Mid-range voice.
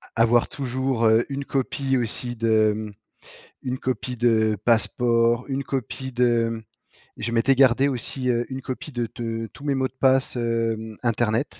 No: low, 120 Hz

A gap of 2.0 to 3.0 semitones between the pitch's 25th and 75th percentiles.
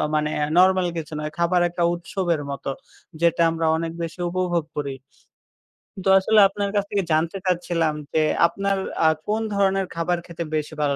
Yes: average, 2.7 semitones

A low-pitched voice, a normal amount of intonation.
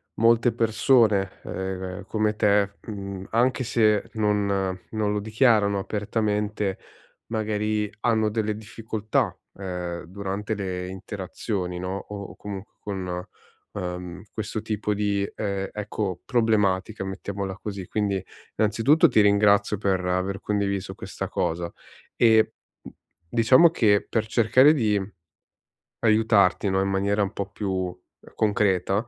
No: low, 105 Hz; narrow, 2.1 semitones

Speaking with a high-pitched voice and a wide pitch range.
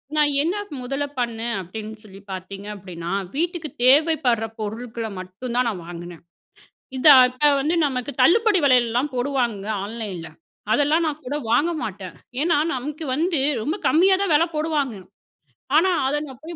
Yes: very high, 255 Hz; wide, 5.8 semitones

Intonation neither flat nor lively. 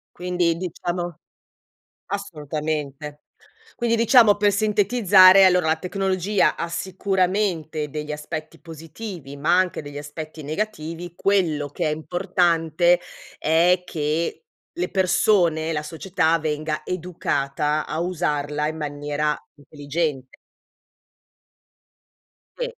Yes: average, 3.6 semitones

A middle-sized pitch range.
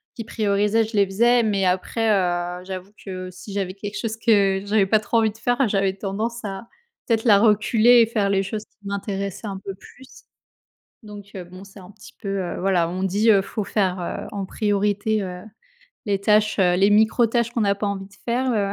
No: narrow, 2.2 semitones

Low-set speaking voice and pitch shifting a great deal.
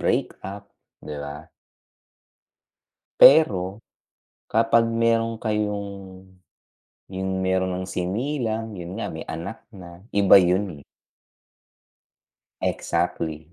No: very low, 95 Hz; average, 4.1 semitones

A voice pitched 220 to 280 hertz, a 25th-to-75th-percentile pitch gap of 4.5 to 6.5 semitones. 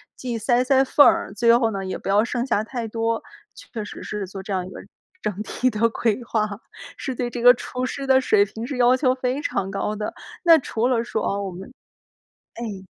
No: high, 230 Hz; average, 3.4 semitones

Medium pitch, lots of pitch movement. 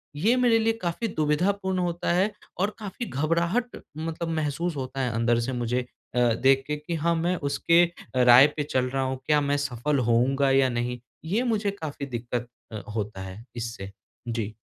Yes: medium, 145 Hz; wide, 5.7 semitones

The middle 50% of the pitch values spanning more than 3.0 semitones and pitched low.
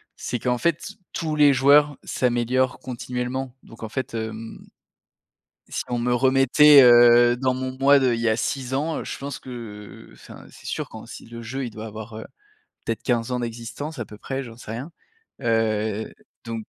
No: average, 2.7 semitones; low, 120 Hz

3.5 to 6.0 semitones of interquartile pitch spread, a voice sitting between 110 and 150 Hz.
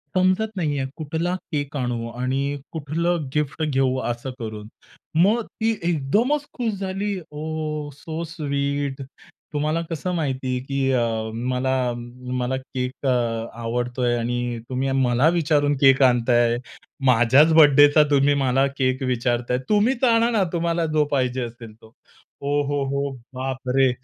Yes: average, 3.9 semitones; medium, 140 Hz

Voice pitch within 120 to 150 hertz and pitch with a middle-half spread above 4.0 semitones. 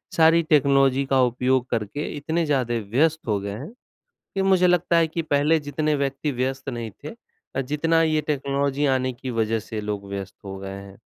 Yes: low, 135 Hz; average, 4.5 semitones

